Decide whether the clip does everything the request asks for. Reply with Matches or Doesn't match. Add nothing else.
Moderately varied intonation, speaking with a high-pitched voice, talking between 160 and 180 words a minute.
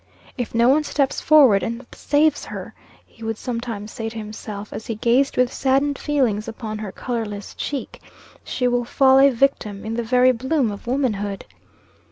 Matches